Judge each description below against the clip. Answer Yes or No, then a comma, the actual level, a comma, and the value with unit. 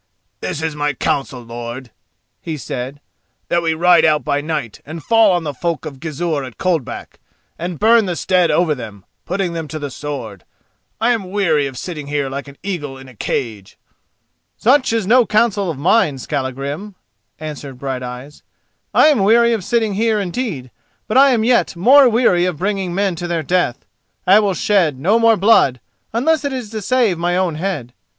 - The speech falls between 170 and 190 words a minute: Yes, average, 185 wpm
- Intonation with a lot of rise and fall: Yes, wide, 6.7 semitones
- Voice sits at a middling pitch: Yes, medium, 170 Hz